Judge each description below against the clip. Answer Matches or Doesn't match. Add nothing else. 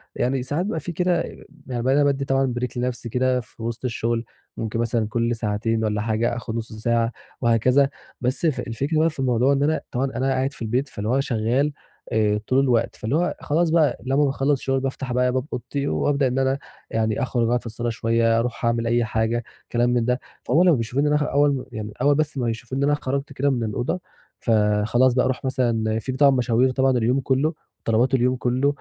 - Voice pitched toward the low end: Matches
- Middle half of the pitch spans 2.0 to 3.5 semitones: Matches